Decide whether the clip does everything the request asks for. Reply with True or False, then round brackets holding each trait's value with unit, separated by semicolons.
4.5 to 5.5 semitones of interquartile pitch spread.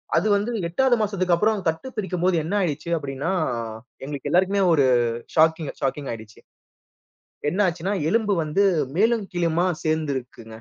True (5.0 semitones)